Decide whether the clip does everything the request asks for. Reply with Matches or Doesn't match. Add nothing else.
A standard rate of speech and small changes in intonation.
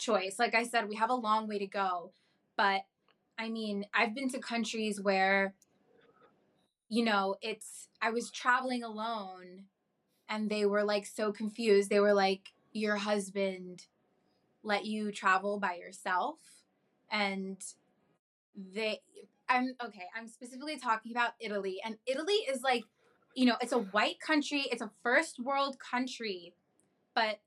Doesn't match